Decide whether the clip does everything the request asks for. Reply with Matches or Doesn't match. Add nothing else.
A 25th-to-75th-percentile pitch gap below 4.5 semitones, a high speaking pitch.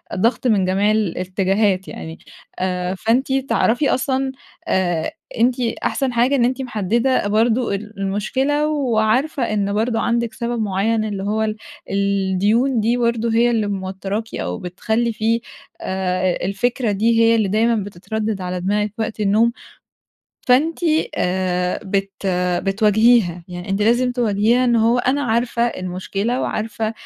Matches